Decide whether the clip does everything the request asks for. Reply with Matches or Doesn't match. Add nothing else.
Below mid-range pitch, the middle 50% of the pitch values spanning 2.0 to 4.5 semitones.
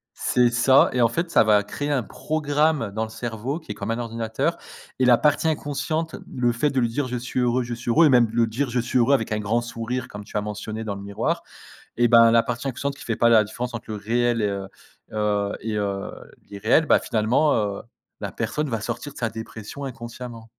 Matches